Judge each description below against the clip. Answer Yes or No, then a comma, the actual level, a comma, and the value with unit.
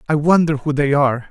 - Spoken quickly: Yes, fast, 230 wpm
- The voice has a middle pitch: Yes, medium, 145 Hz